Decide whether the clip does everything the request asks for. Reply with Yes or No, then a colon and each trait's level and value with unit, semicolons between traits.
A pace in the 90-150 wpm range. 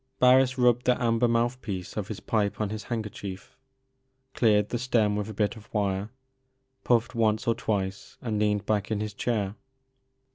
No: average, 175 wpm